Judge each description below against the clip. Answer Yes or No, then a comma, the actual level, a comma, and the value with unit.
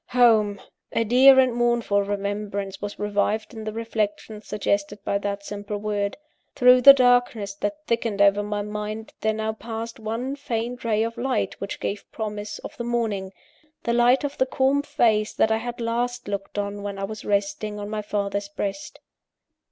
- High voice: Yes, high, 215 Hz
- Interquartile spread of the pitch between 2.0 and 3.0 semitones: Yes, average, 2.7 semitones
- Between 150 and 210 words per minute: Yes, average, 180 wpm